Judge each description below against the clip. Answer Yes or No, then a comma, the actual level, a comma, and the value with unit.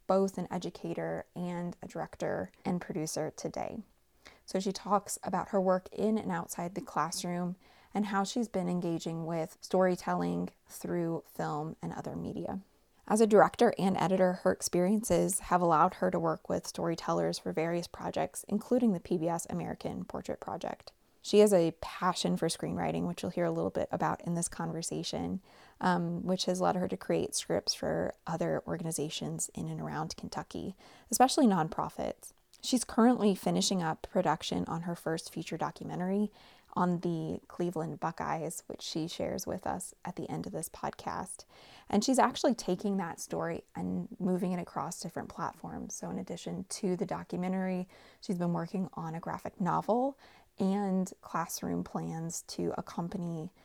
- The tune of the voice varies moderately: Yes, average, 3.3 semitones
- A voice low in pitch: No, medium, 180 Hz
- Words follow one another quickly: No, average, 160 wpm